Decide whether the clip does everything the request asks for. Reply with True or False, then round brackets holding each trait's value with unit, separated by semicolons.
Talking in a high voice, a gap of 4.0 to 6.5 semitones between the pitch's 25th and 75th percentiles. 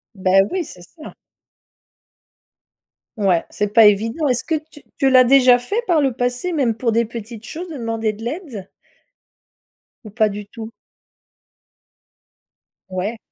True (235 Hz; 4.3 semitones)